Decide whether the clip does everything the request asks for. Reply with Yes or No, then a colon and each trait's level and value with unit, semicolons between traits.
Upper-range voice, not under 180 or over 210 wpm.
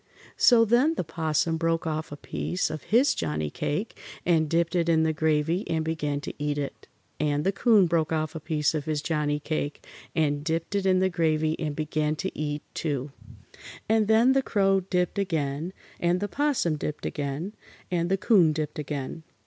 No: medium, 160 Hz; average, 190 wpm